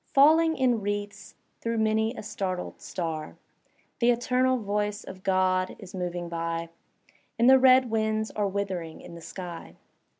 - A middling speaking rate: Yes, average, 145 wpm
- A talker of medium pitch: No, high, 205 Hz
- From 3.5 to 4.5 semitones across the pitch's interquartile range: Yes, average, 4.2 semitones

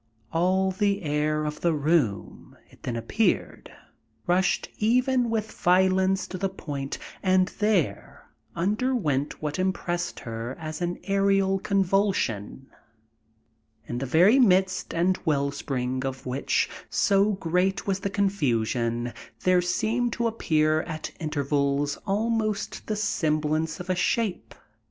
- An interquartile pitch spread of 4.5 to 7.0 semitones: Yes, average, 5.0 semitones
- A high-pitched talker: No, medium, 180 Hz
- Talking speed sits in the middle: No, slow, 125 wpm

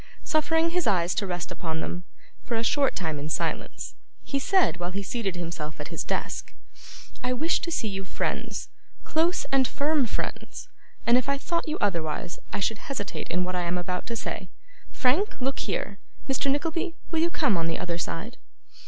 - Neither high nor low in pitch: No, high, 230 Hz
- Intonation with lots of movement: Yes, wide, 8.7 semitones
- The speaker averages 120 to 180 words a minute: No, average, 190 wpm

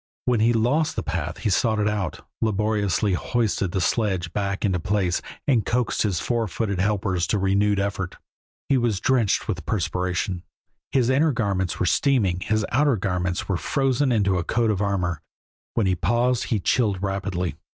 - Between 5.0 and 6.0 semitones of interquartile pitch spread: No, average, 3.9 semitones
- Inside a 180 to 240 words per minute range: No, average, 170 wpm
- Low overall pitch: Yes, low, 100 Hz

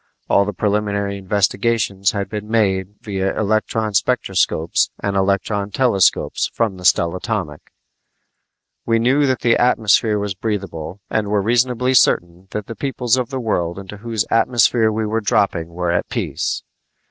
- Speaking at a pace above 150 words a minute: No, average, 140 wpm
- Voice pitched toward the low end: Yes, low, 105 Hz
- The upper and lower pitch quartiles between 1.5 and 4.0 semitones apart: Yes, average, 2.9 semitones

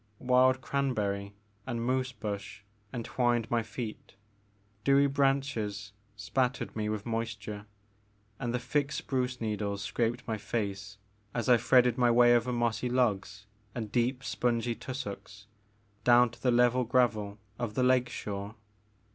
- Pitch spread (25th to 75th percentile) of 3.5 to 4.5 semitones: No, average, 3.0 semitones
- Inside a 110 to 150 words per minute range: Yes, slow, 135 wpm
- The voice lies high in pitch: No, low, 120 Hz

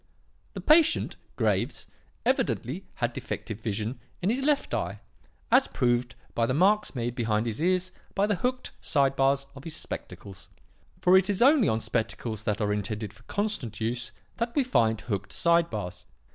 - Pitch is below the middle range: Yes, low, 130 Hz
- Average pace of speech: Yes, average, 170 wpm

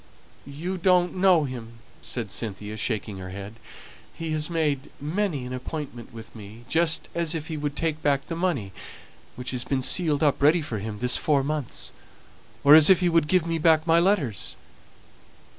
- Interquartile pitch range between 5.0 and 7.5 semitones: Yes, wide, 5.5 semitones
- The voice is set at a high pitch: No, medium, 145 Hz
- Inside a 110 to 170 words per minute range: No, average, 180 wpm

